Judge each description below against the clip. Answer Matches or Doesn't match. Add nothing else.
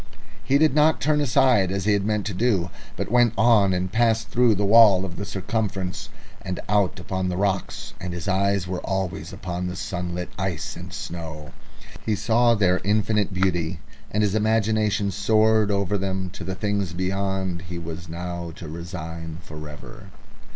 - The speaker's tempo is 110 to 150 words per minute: Doesn't match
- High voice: Doesn't match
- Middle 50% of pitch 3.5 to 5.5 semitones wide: Doesn't match